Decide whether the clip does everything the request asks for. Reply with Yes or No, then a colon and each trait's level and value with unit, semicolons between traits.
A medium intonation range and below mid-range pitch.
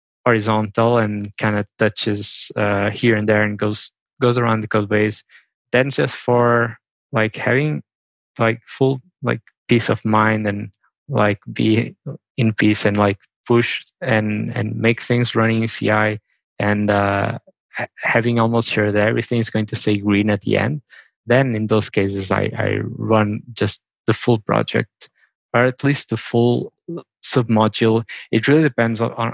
No: narrow, 2.1 semitones; low, 110 Hz